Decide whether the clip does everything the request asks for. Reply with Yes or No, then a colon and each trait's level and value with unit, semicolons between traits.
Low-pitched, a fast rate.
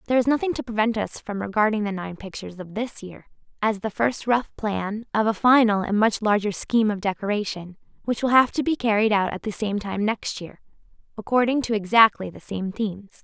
No: high, 215 Hz; fast, 215 wpm